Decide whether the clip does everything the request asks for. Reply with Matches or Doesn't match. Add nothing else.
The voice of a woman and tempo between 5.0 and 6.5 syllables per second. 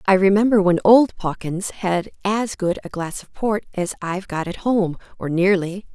Doesn't match